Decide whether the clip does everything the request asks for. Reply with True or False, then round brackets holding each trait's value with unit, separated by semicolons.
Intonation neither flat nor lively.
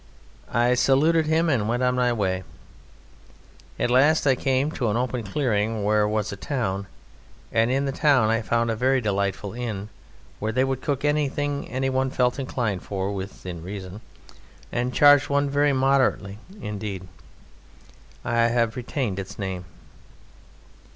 True (4.6 semitones)